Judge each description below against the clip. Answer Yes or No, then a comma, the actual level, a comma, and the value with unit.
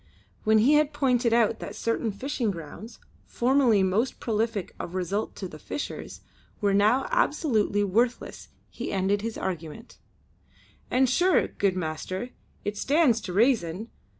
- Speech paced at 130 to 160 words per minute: Yes, average, 140 wpm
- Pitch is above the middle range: Yes, high, 220 Hz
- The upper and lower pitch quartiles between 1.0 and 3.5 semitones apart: No, average, 4.3 semitones